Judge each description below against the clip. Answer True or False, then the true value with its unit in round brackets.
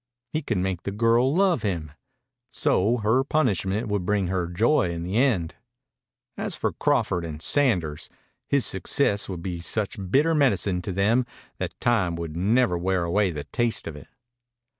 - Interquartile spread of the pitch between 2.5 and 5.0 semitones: False (5.4 semitones)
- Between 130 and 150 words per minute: False (165 wpm)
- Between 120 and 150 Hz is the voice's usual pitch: False (100 Hz)